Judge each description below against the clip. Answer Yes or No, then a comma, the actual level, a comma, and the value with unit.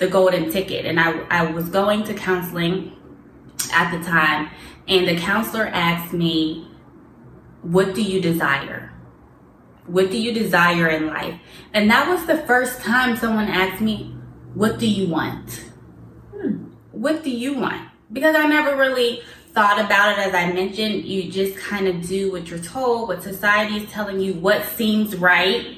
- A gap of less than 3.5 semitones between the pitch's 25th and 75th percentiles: No, average, 4.0 semitones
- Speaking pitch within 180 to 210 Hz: Yes, high, 190 Hz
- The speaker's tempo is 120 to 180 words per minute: Yes, average, 170 wpm